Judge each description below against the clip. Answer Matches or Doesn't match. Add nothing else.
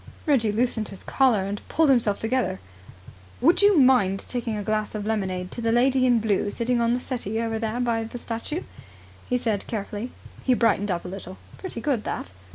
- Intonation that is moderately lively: Matches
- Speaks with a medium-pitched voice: Doesn't match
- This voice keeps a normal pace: Matches